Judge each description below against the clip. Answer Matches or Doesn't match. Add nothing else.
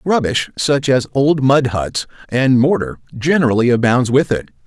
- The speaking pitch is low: Matches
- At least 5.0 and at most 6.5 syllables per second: Doesn't match